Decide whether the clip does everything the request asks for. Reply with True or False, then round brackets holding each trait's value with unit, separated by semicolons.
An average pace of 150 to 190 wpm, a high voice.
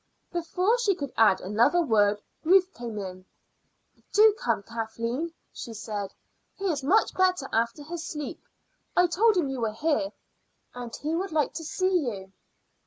True (160 wpm; 290 Hz)